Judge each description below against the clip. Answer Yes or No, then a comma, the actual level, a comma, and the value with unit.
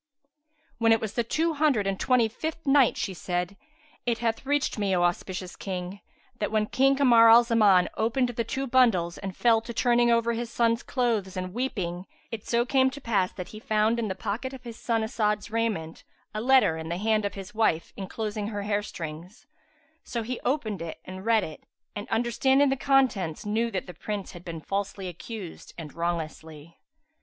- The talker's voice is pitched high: Yes, high, 220 Hz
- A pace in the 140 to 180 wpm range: No, average, 190 wpm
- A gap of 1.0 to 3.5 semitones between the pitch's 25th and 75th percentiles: No, average, 4.1 semitones